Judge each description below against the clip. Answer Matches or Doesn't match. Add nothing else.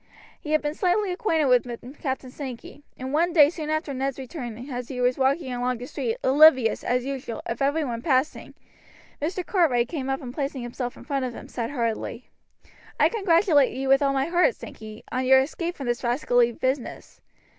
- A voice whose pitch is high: Matches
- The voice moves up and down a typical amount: Matches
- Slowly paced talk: Doesn't match